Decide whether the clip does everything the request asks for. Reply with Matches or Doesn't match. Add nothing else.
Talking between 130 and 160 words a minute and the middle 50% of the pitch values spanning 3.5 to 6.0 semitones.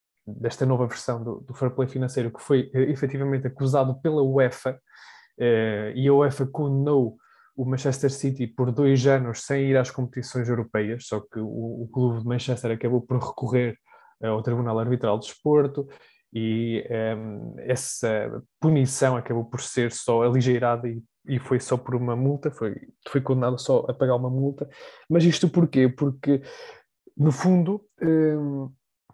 Doesn't match